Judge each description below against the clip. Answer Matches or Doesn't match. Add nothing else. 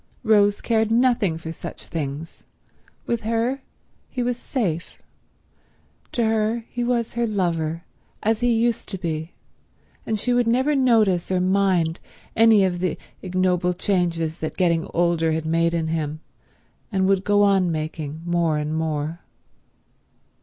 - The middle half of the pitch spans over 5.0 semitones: Matches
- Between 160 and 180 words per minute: Doesn't match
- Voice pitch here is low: Doesn't match